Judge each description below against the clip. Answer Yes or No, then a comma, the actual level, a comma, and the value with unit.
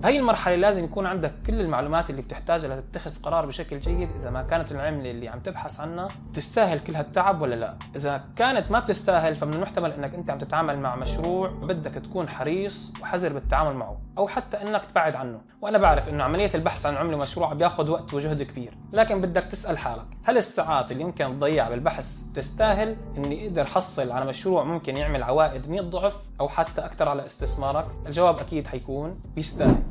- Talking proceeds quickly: Yes, fast, 185 wpm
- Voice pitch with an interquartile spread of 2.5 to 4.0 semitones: No, wide, 5.4 semitones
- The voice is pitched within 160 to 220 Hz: Yes, medium, 165 Hz